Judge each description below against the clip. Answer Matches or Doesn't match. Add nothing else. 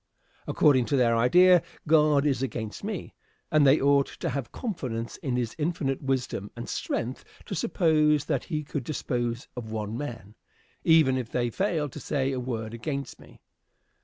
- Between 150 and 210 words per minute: Matches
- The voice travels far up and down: Doesn't match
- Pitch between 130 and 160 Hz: Matches